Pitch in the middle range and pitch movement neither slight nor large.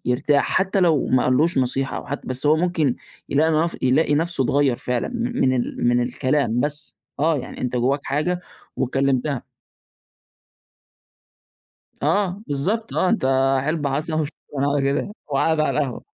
Yes: medium, 145 Hz; average, 3.7 semitones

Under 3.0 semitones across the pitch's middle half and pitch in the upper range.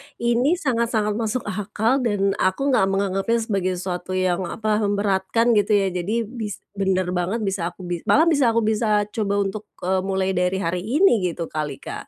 No: average, 3.5 semitones; high, 200 Hz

